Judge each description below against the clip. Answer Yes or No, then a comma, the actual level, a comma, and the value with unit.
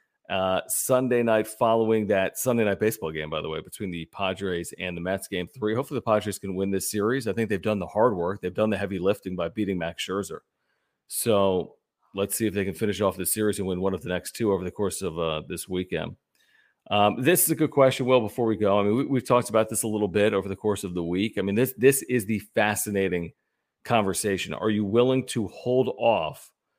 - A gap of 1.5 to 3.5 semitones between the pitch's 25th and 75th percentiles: Yes, average, 2.9 semitones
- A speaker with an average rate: No, fast, 240 wpm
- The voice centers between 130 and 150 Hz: No, low, 105 Hz